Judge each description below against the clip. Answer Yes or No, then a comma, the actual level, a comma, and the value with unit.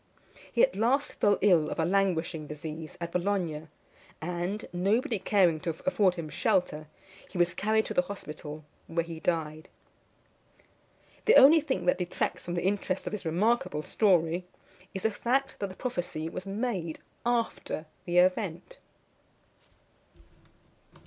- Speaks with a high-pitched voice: No, medium, 180 Hz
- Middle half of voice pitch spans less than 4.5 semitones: Yes, average, 4.1 semitones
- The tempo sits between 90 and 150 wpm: Yes, average, 140 wpm